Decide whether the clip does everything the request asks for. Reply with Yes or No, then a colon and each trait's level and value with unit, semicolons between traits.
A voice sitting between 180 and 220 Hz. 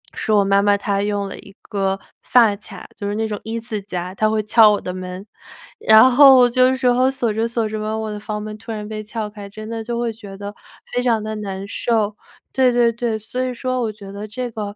Yes: high, 215 Hz